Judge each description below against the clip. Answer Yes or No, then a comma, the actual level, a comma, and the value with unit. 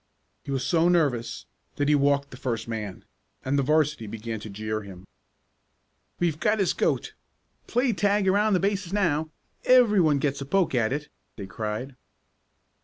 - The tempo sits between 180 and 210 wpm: No, average, 165 wpm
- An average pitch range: No, wide, 8.1 semitones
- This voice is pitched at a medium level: Yes, medium, 145 Hz